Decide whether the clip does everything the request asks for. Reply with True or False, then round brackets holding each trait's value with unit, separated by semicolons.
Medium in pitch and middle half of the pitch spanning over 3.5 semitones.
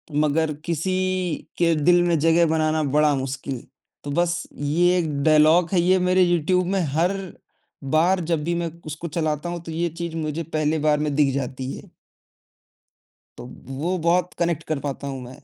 False (160 Hz; 2.7 semitones)